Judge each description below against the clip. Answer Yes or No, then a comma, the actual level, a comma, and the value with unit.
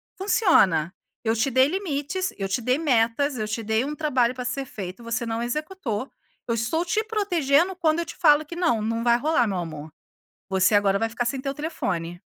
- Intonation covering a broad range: Yes, wide, 6.0 semitones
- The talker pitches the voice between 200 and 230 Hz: No, very high, 250 Hz